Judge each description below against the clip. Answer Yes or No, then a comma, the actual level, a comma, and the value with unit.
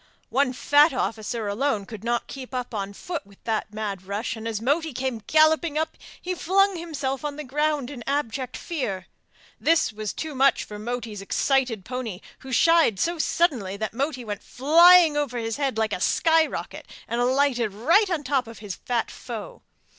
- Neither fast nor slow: Yes, average, 185 wpm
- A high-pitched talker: Yes, very high, 255 Hz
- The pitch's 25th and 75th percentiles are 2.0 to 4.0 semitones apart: No, wide, 5.4 semitones